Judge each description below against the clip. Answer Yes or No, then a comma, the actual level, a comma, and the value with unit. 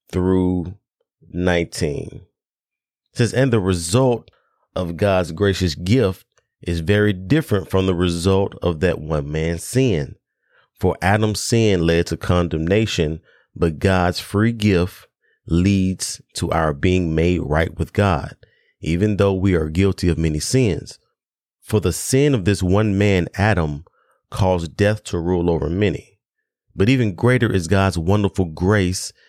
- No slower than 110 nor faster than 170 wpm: Yes, average, 140 wpm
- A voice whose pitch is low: Yes, very low, 95 Hz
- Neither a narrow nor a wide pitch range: Yes, average, 3.2 semitones